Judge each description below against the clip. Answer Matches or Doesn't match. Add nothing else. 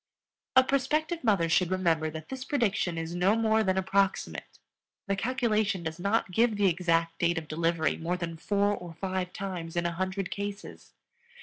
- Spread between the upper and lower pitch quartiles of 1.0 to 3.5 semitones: Doesn't match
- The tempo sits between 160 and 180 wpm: Matches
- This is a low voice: Doesn't match